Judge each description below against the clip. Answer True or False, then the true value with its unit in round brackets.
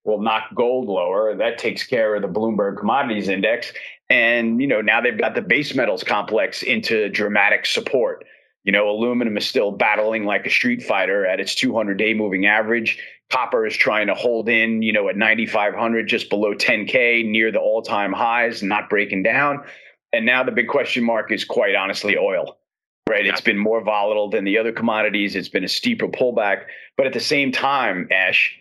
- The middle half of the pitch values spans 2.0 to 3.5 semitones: True (2.4 semitones)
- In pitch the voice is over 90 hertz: True (110 Hz)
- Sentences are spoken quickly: False (190 wpm)